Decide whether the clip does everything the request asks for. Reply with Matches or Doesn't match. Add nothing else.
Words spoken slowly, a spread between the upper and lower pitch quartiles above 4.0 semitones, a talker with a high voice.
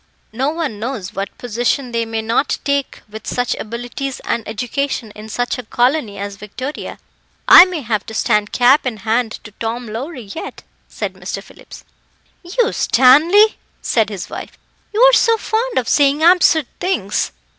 Doesn't match